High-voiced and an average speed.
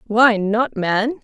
Yes: high, 225 Hz; average, 145 wpm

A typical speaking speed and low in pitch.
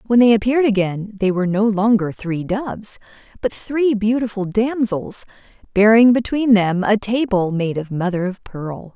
No: average, 160 wpm; high, 210 Hz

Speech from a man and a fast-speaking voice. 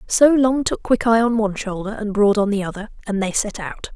No: female; fast, 245 wpm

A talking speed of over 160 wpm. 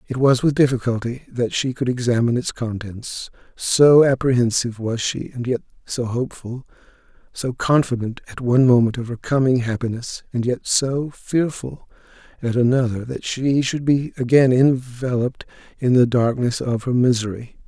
No: average, 155 wpm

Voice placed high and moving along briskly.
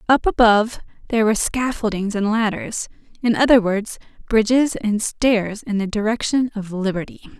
No: high, 220 Hz; average, 145 wpm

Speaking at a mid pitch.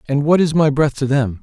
Yes: medium, 145 Hz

